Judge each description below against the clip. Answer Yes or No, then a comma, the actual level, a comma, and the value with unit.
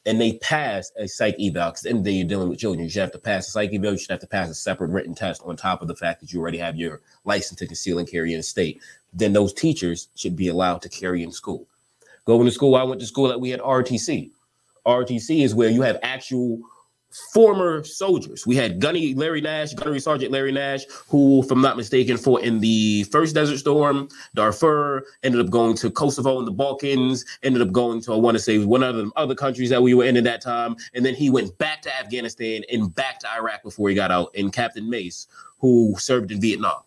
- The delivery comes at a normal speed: No, fast, 245 wpm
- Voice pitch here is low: Yes, low, 120 Hz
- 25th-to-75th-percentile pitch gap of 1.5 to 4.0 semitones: No, average, 4.7 semitones